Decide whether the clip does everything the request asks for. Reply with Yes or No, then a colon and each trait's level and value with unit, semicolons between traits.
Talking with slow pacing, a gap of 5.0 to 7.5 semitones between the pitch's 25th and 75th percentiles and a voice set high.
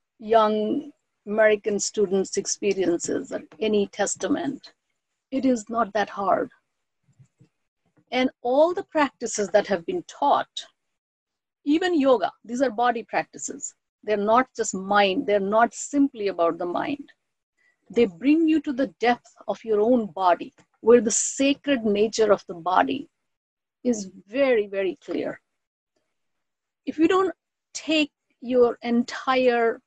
Yes: slow, 125 wpm; average, 5.3 semitones; high, 235 Hz